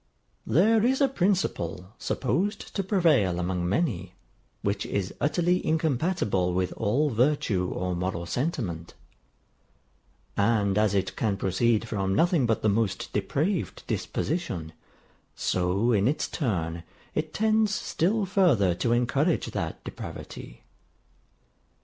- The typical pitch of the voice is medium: No, low, 115 Hz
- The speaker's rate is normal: No, slow, 120 wpm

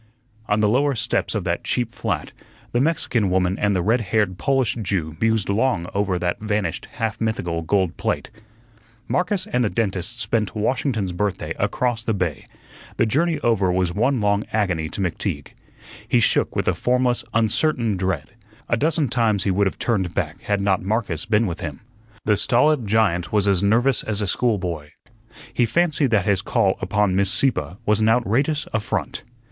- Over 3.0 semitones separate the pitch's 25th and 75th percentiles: Yes, average, 4.1 semitones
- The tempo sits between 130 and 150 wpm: No, average, 175 wpm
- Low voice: Yes, low, 105 Hz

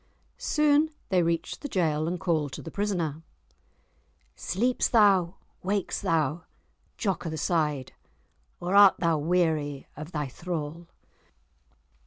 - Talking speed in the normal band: No, slow, 125 wpm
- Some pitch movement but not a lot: Yes, average, 3.7 semitones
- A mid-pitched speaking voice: Yes, medium, 170 Hz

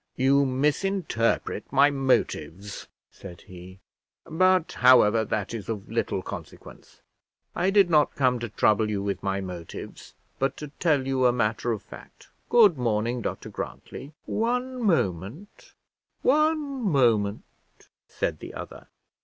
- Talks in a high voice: No, low, 130 Hz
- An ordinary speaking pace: No, slow, 130 wpm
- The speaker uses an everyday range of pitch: No, wide, 7.9 semitones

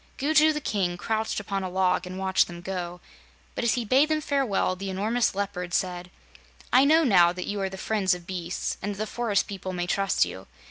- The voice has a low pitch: No, high, 195 Hz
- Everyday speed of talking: No, fast, 220 wpm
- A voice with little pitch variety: No, average, 3.8 semitones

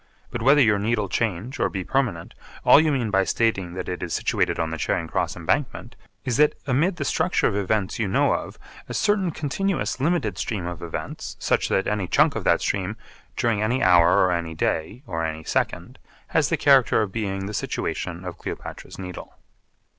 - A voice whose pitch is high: No, low, 105 Hz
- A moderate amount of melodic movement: No, wide, 6.3 semitones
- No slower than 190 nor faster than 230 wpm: Yes, average, 195 wpm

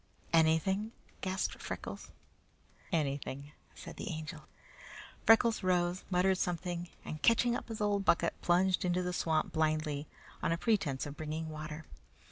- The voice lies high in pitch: No, medium, 175 Hz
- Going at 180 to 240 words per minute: No, slow, 135 wpm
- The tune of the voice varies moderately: Yes, average, 3.5 semitones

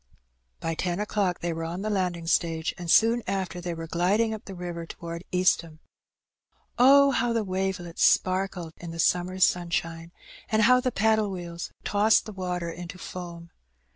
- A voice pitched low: No, medium, 180 Hz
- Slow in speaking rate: No, average, 170 wpm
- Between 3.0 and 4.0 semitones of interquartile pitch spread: Yes, average, 3.4 semitones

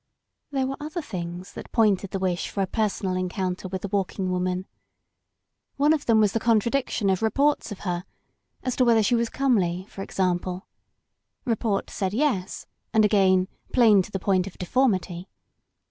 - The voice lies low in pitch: No, high, 200 Hz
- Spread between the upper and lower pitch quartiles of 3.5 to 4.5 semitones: Yes, average, 4.0 semitones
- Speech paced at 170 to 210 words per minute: Yes, average, 175 wpm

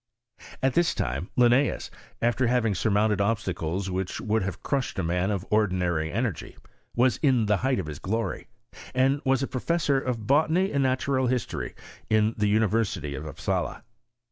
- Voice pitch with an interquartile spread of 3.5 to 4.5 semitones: No, wide, 5.5 semitones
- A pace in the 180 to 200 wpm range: No, average, 160 wpm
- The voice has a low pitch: Yes, low, 110 Hz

